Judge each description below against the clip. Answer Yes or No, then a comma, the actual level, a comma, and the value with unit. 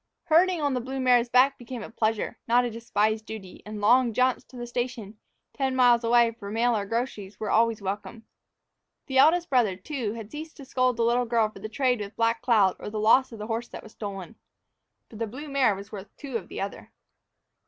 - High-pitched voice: Yes, high, 235 Hz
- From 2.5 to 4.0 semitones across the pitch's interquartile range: Yes, average, 3.0 semitones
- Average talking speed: No, fast, 220 wpm